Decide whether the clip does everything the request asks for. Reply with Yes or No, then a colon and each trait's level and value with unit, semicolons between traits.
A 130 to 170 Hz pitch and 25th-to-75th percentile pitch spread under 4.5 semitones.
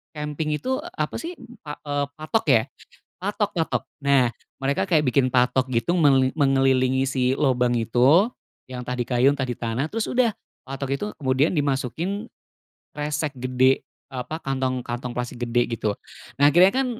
Yes: low, 135 Hz; average, 3.5 semitones